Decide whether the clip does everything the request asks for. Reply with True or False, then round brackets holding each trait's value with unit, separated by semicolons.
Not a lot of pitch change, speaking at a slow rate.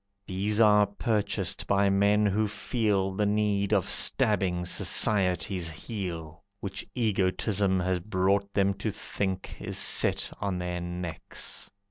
True (2.1 semitones; 125 wpm)